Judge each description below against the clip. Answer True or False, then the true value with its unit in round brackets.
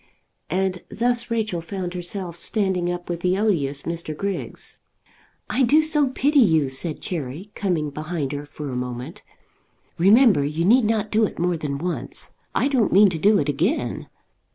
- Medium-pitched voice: True (180 Hz)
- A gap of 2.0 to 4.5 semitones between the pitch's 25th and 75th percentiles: False (5.6 semitones)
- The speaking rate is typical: True (170 wpm)